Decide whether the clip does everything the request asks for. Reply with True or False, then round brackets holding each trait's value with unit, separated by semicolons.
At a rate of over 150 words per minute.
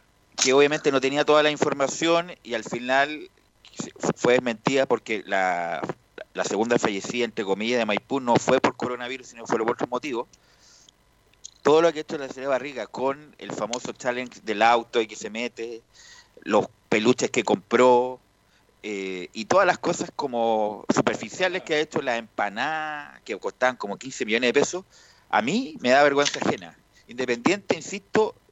True (170 wpm)